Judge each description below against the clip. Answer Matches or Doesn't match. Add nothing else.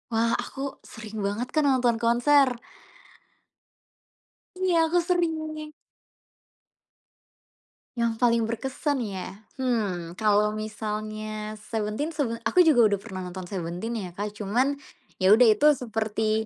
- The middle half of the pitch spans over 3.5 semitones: Matches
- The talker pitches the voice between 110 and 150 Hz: Doesn't match